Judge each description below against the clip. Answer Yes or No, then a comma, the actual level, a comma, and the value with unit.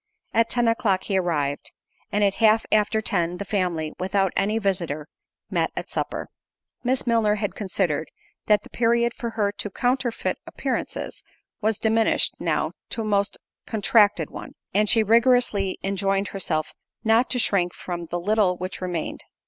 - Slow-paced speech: No, average, 155 wpm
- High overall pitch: Yes, high, 205 Hz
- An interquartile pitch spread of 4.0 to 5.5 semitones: No, average, 3.4 semitones